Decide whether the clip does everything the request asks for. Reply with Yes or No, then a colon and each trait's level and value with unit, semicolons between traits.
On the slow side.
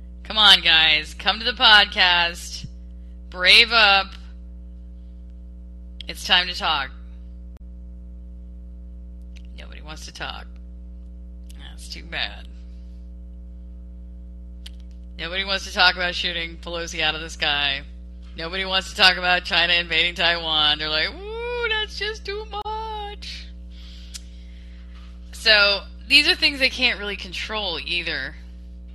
Yes: slow, 115 wpm